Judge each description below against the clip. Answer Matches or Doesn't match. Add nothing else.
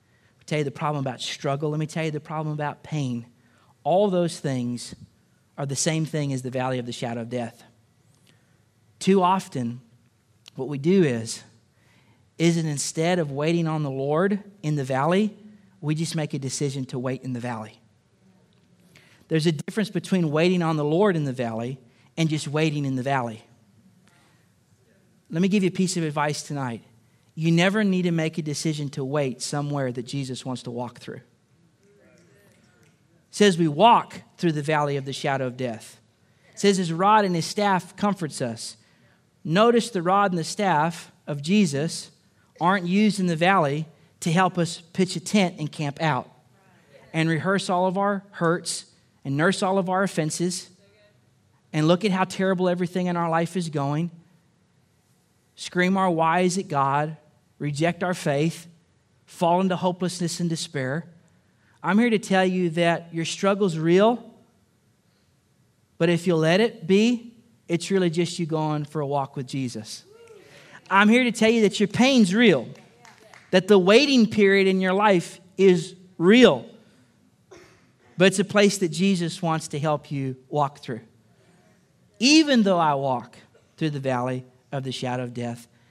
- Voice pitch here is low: Doesn't match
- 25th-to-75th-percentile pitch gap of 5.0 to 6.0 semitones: Matches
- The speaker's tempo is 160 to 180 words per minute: Matches